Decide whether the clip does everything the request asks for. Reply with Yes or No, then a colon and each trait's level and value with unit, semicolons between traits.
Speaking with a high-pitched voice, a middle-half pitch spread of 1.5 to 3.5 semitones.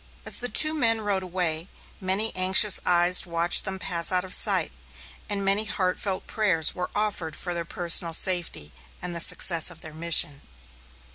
No: medium, 180 Hz; average, 2.7 semitones